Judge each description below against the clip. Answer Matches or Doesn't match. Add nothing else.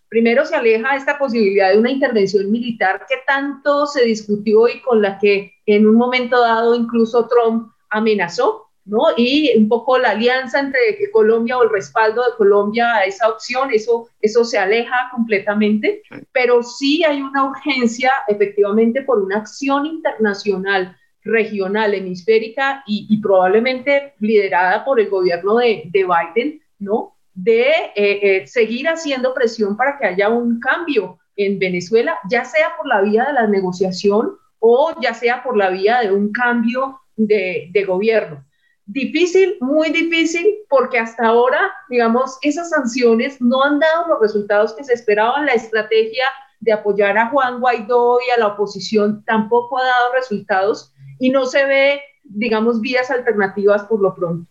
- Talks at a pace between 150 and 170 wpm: Matches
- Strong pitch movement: Doesn't match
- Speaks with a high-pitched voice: Matches